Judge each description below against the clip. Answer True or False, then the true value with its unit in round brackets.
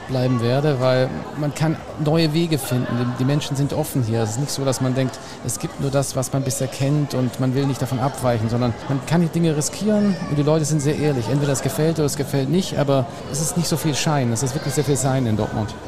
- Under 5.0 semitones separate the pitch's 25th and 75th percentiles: True (2.9 semitones)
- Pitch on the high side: False (140 Hz)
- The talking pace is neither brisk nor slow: False (255 wpm)